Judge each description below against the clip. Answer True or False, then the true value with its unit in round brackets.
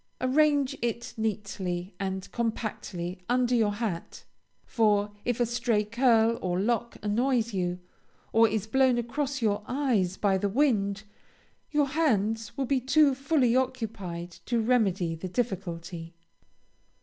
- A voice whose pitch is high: True (225 Hz)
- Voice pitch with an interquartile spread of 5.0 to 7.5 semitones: False (4.4 semitones)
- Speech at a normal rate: False (130 wpm)